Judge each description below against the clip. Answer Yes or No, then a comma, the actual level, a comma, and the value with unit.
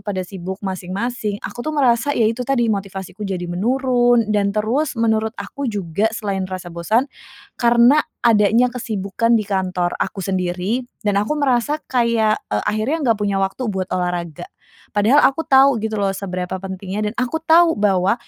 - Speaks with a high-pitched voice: Yes, high, 210 Hz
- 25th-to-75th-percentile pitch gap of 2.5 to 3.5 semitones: No, average, 4.1 semitones